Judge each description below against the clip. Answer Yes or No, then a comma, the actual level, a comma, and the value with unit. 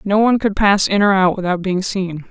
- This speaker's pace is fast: Yes, fast, 260 wpm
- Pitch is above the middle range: Yes, high, 195 Hz